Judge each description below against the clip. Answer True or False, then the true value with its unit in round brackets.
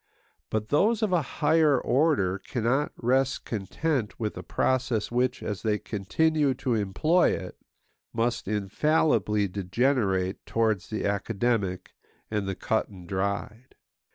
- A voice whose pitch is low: True (115 Hz)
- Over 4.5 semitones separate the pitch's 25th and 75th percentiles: True (5.0 semitones)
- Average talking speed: False (125 wpm)